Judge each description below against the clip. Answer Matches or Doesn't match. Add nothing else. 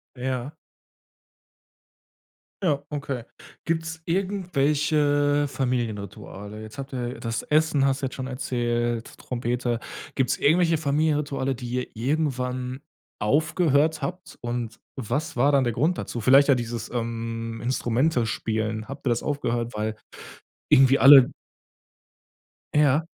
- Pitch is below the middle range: Matches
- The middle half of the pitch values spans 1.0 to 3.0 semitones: Doesn't match